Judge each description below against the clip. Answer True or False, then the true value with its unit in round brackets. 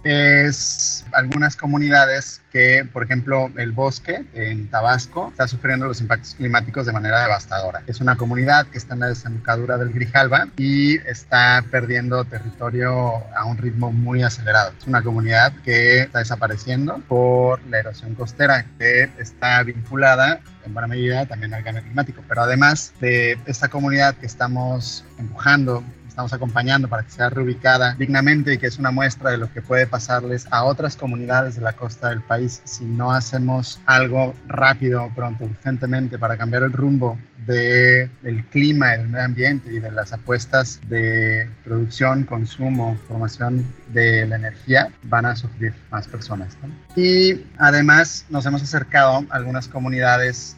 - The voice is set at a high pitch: False (125 Hz)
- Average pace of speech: True (155 wpm)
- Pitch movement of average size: False (2.2 semitones)